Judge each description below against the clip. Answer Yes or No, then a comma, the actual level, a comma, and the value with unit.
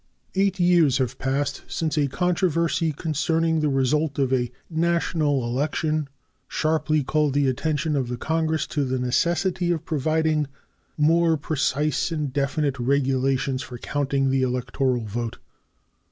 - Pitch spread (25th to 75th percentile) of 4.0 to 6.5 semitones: No, average, 3.2 semitones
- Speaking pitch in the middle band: Yes, medium, 150 Hz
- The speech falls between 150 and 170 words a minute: No, slow, 135 wpm